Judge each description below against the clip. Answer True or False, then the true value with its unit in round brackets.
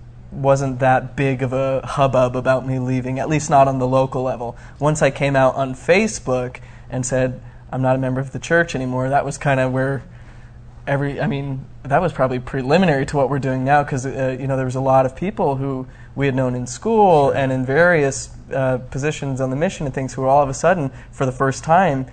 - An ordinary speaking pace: False (230 wpm)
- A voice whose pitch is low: True (130 Hz)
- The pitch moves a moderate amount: False (1.4 semitones)